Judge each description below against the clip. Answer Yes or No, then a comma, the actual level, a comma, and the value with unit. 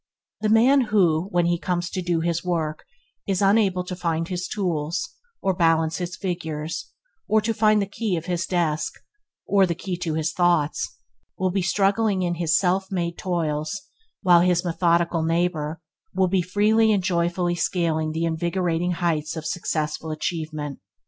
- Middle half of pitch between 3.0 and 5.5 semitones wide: No, narrow, 2.5 semitones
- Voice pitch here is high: No, medium, 175 Hz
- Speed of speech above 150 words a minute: Yes, average, 170 wpm